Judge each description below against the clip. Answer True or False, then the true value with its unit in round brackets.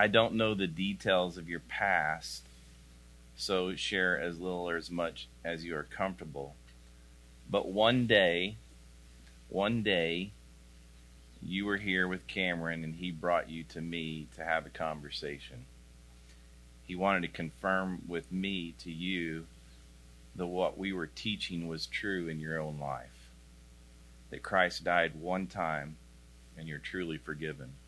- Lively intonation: True (7.2 semitones)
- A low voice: True (80 Hz)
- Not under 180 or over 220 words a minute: False (145 wpm)